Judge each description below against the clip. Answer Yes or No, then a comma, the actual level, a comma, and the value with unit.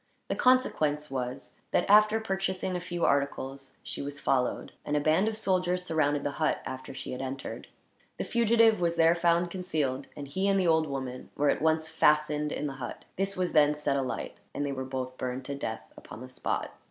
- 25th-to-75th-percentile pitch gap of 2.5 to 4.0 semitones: No, average, 4.9 semitones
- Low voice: No, medium, 150 Hz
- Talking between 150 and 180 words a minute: No, average, 200 wpm